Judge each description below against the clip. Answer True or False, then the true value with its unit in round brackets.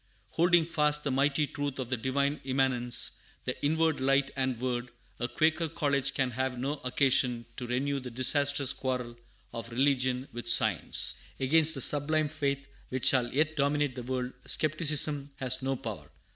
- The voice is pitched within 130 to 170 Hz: True (135 Hz)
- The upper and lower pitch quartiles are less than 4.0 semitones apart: True (2.5 semitones)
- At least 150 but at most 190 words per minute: True (160 wpm)